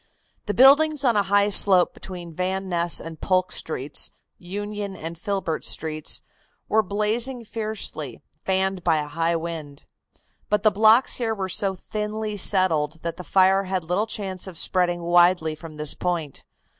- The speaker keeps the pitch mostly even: No, average, 3.8 semitones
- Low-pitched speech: No, medium, 185 Hz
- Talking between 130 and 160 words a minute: Yes, average, 155 wpm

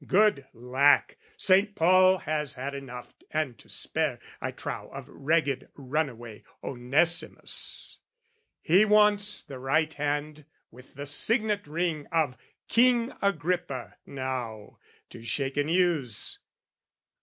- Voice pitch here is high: No, medium, 150 Hz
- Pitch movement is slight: No, wide, 5.4 semitones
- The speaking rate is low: Yes, slow, 120 wpm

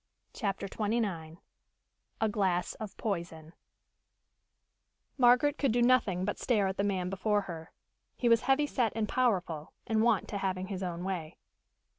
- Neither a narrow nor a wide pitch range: Yes, average, 4.2 semitones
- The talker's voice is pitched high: Yes, high, 200 Hz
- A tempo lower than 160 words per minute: Yes, average, 150 wpm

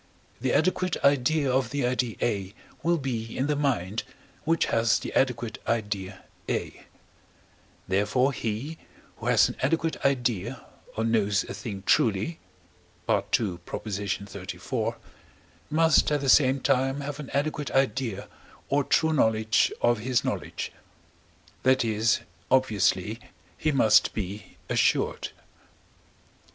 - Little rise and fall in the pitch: No, average, 4.8 semitones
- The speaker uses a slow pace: Yes, slow, 120 wpm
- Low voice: Yes, low, 125 Hz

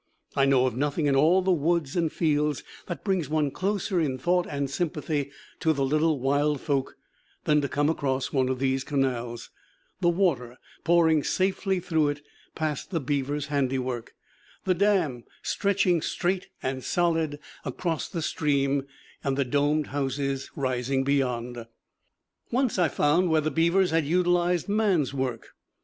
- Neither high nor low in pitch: Yes, medium, 150 Hz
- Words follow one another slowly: No, average, 155 wpm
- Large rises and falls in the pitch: No, average, 4.1 semitones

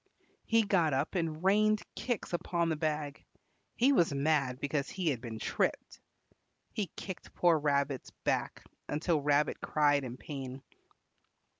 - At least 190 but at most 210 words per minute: No, average, 140 wpm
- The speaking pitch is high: No, medium, 155 Hz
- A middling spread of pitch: Yes, average, 3.9 semitones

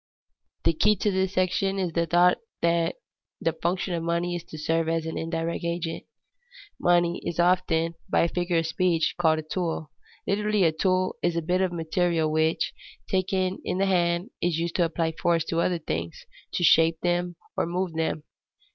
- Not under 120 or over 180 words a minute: No, average, 190 wpm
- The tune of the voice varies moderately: No, narrow, 1.8 semitones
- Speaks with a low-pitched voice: No, medium, 170 Hz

